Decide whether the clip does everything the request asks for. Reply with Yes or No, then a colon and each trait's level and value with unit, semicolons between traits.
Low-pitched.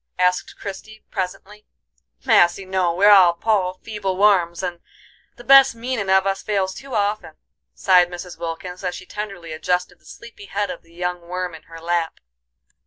No: medium, 185 Hz